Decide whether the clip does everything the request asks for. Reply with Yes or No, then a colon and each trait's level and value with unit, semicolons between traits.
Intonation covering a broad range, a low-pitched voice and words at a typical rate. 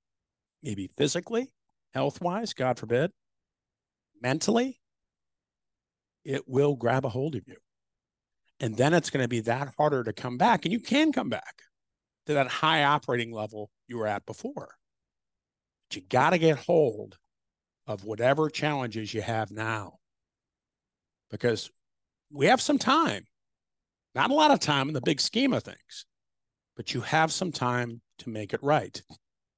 Yes: wide, 6.2 semitones; low, 125 Hz; average, 155 wpm